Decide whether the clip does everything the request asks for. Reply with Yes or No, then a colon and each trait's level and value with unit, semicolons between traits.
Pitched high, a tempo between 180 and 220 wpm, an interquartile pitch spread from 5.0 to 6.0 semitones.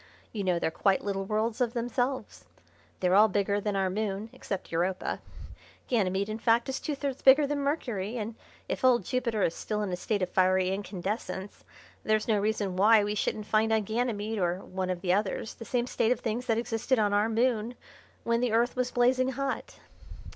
No: high, 215 Hz; average, 200 wpm; average, 3.7 semitones